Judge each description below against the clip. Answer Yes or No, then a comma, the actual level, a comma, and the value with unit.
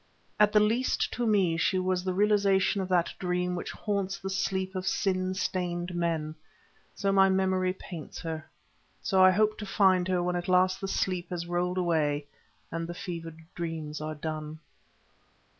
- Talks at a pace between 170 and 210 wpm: Yes, average, 175 wpm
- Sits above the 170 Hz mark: Yes, medium, 185 Hz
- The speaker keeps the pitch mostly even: Yes, narrow, 2.0 semitones